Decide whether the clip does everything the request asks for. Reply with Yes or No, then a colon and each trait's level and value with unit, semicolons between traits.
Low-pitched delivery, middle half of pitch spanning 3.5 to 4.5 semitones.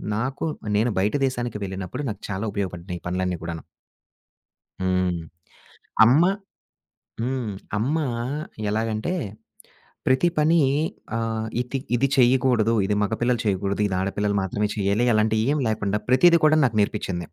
Yes: low, 110 Hz; average, 4.2 semitones